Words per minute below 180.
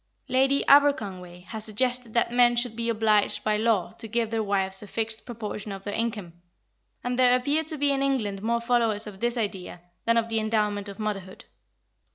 No: average, 195 wpm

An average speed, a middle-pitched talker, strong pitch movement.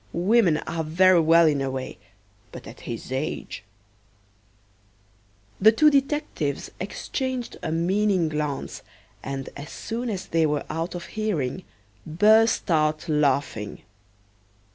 No: slow, 125 wpm; medium, 160 Hz; wide, 6.8 semitones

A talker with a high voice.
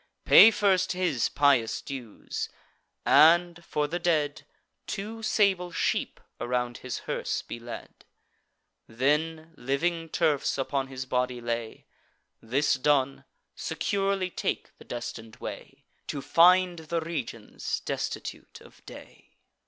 No: medium, 150 Hz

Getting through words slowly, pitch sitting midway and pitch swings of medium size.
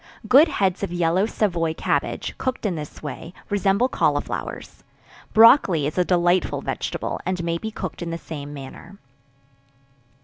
No: average, 145 wpm; medium, 175 Hz; average, 3.6 semitones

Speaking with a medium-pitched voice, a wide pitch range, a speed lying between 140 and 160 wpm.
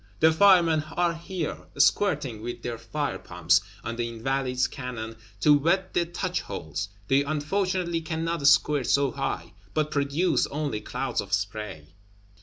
Yes: medium, 145 Hz; wide, 6.2 semitones; average, 145 wpm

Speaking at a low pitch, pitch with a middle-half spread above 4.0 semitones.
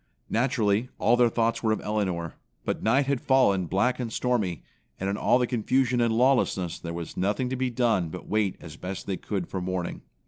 Yes: low, 110 Hz; average, 5.0 semitones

